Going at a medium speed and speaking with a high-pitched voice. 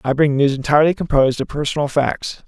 No: average, 195 wpm; medium, 145 Hz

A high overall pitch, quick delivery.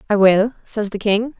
Yes: high, 210 Hz; fast, 215 wpm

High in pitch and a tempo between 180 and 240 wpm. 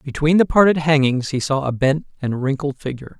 No: medium, 145 Hz; fast, 205 wpm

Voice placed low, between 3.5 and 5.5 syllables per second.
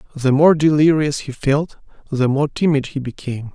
No: medium, 145 Hz; 5.1 syllables/s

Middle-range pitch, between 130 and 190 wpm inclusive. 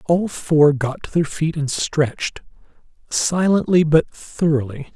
Yes: medium, 155 Hz; slow, 135 wpm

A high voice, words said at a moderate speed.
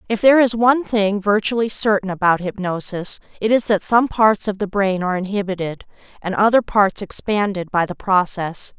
Yes: high, 200 Hz; average, 180 wpm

